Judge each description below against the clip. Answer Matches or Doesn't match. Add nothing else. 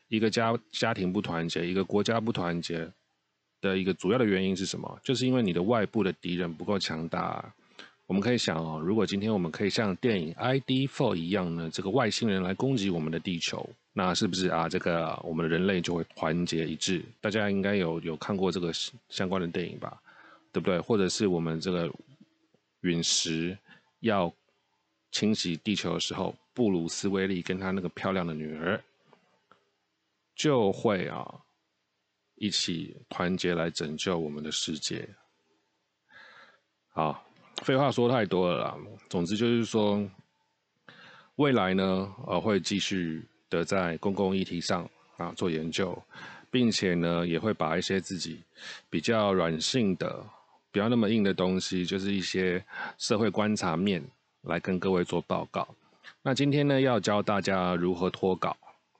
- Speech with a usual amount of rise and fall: Matches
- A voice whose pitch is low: Matches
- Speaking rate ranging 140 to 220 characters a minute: Doesn't match